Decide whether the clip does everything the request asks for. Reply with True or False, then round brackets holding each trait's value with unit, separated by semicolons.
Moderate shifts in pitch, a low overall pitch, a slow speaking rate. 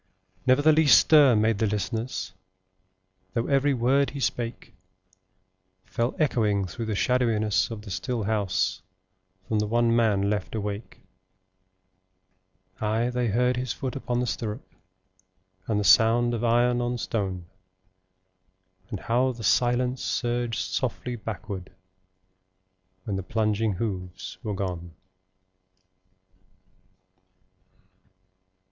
True (3.1 semitones; 115 Hz; 115 wpm)